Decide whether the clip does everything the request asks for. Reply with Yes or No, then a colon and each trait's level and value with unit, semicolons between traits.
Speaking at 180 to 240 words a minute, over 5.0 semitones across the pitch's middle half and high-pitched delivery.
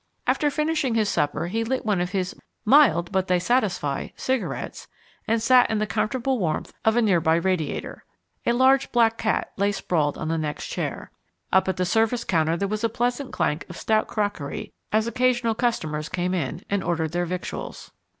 Yes: average, 190 wpm; wide, 5.4 semitones; high, 205 Hz